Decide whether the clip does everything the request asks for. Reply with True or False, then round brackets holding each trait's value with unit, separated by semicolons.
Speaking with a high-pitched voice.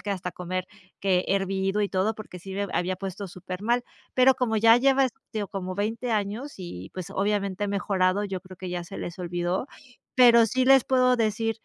True (200 Hz)